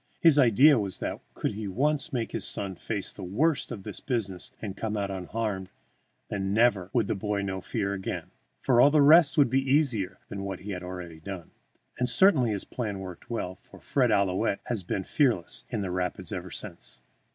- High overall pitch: No, low, 100 Hz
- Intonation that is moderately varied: Yes, average, 4.8 semitones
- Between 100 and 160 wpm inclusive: No, average, 200 wpm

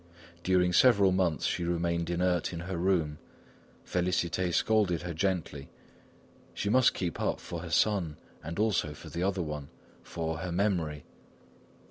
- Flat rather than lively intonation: Yes, narrow, 2.1 semitones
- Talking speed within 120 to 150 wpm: Yes, average, 145 wpm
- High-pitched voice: No, very low, 90 Hz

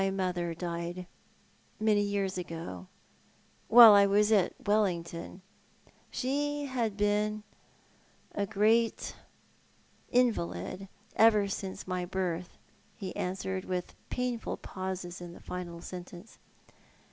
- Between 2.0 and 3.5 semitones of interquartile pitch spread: Yes, average, 3.2 semitones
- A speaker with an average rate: No, slow, 110 wpm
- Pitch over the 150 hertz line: Yes, high, 190 Hz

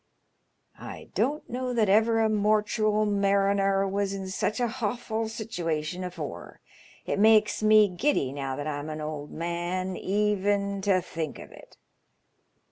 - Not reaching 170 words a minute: Yes, average, 140 wpm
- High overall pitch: Yes, high, 200 Hz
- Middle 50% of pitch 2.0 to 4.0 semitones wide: Yes, average, 3.7 semitones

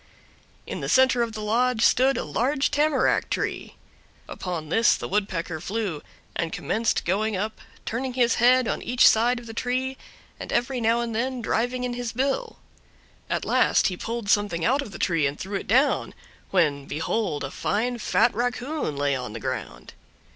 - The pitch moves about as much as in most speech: Yes, average, 5.0 semitones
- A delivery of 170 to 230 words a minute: Yes, average, 180 wpm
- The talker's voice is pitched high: Yes, high, 230 Hz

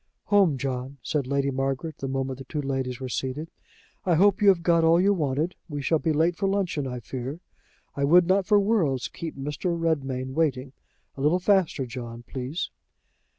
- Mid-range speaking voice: Yes, medium, 145 Hz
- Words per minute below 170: No, average, 190 wpm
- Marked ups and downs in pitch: No, average, 4.5 semitones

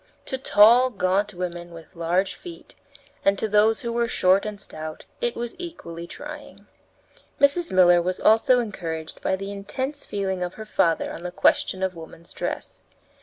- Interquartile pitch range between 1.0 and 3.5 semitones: No, average, 4.9 semitones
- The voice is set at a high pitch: Yes, high, 195 Hz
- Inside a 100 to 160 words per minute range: No, average, 170 wpm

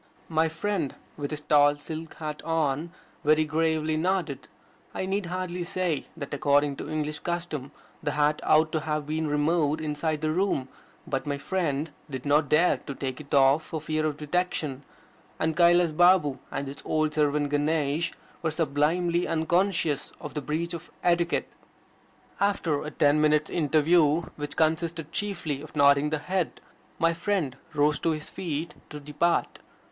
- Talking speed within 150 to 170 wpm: Yes, average, 160 wpm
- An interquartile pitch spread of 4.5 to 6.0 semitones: No, narrow, 2.4 semitones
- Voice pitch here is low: No, medium, 155 Hz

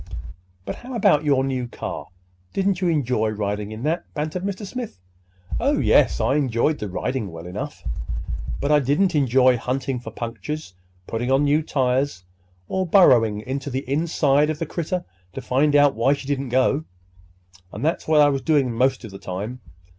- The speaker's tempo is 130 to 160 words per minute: No, average, 175 wpm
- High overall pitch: No, low, 135 Hz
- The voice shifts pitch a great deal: No, average, 4.2 semitones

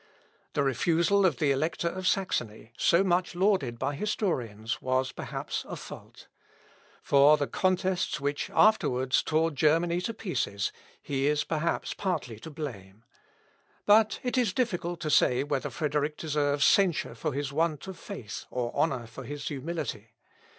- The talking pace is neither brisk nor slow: Yes, average, 150 wpm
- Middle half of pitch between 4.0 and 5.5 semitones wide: Yes, average, 5.0 semitones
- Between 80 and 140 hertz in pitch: No, medium, 150 Hz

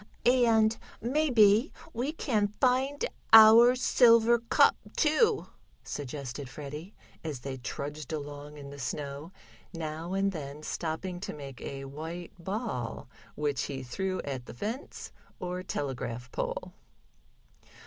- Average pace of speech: No, slow, 120 wpm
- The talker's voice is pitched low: No, medium, 170 Hz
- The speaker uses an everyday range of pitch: No, wide, 8.0 semitones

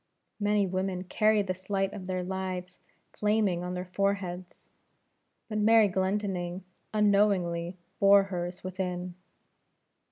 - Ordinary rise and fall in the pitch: No, narrow, 1.9 semitones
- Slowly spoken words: Yes, slow, 115 wpm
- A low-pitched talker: No, high, 190 Hz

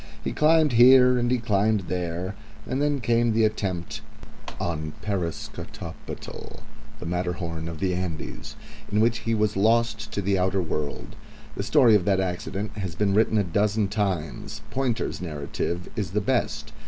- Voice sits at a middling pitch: No, low, 100 Hz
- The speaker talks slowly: No, average, 155 wpm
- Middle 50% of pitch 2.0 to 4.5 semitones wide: Yes, average, 4.2 semitones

